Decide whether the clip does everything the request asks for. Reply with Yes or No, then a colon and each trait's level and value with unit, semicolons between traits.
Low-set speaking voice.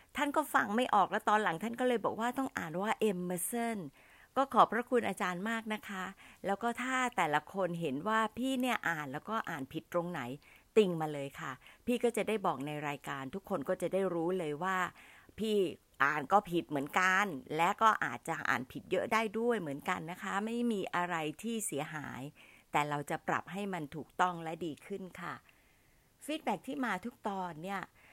No: high, 190 Hz